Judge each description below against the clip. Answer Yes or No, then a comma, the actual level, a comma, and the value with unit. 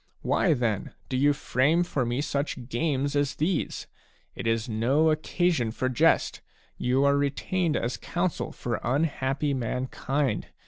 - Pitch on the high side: No, medium, 140 Hz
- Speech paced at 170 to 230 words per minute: No, average, 140 wpm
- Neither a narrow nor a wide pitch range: Yes, average, 3.5 semitones